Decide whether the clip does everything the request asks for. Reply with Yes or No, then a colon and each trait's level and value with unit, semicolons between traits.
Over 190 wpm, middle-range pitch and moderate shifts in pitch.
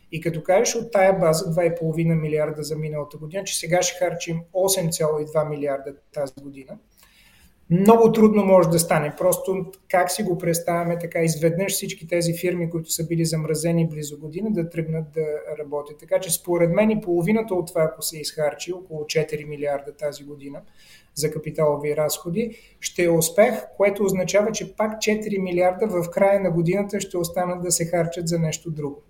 No: average, 175 wpm; medium, 170 Hz; average, 3.2 semitones